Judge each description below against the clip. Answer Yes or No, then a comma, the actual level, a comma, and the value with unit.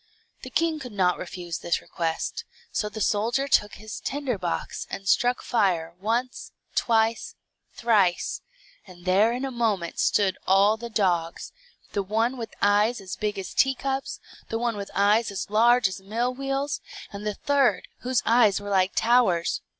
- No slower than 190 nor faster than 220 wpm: No, average, 165 wpm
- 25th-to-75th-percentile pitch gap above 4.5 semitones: No, average, 4.0 semitones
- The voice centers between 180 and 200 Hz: No, high, 215 Hz